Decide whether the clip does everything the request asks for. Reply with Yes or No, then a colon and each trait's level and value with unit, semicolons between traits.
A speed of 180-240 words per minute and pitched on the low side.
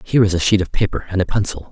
No: fast, 315 wpm; very low, 95 Hz